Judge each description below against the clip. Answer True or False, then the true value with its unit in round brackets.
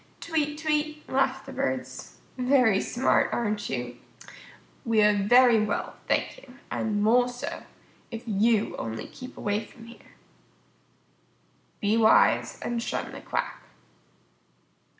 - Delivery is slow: True (125 wpm)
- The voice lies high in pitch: True (235 Hz)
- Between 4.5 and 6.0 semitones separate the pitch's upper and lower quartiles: False (3.9 semitones)